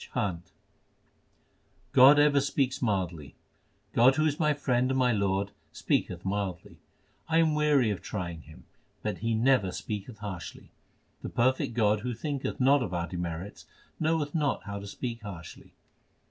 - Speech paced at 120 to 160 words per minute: Yes, average, 150 wpm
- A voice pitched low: Yes, low, 115 Hz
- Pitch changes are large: Yes, wide, 6.1 semitones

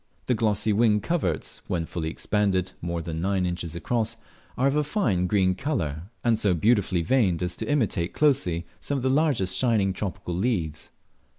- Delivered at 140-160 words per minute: No, average, 175 wpm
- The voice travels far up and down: Yes, wide, 5.7 semitones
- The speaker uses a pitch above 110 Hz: No, low, 100 Hz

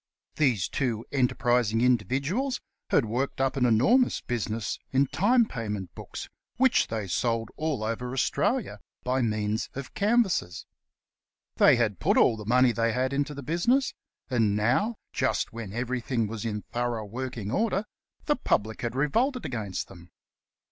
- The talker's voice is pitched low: Yes, low, 125 Hz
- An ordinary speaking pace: Yes, average, 150 wpm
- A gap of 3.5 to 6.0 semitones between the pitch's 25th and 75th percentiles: Yes, average, 4.2 semitones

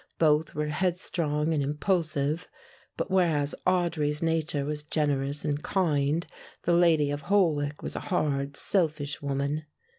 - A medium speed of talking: No, slow, 130 wpm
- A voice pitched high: No, medium, 150 Hz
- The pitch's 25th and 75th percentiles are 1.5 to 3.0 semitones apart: Yes, narrow, 2.6 semitones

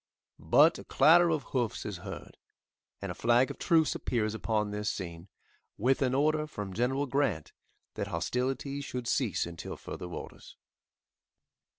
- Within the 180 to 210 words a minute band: No, average, 150 wpm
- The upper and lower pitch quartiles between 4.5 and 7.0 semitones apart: Yes, average, 5.2 semitones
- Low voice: Yes, low, 125 Hz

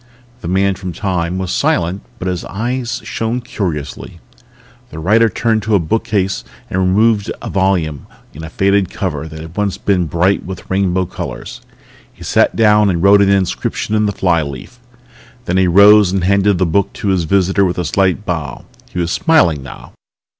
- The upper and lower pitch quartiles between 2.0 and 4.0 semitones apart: Yes, average, 2.9 semitones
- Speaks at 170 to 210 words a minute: Yes, average, 180 wpm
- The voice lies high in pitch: No, very low, 95 Hz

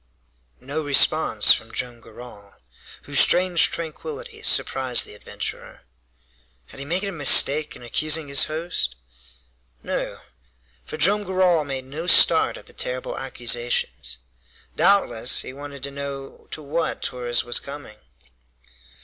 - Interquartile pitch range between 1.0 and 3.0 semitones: No, average, 4.9 semitones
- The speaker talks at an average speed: No, slow, 130 wpm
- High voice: No, medium, 140 Hz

